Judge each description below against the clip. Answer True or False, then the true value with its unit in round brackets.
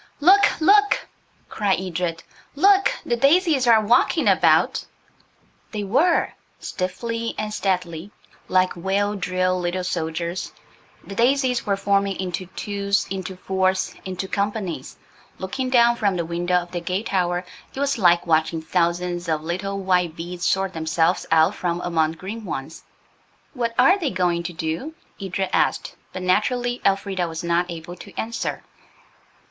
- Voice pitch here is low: False (185 Hz)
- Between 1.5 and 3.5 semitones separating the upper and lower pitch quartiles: False (4.1 semitones)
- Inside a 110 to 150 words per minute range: True (145 wpm)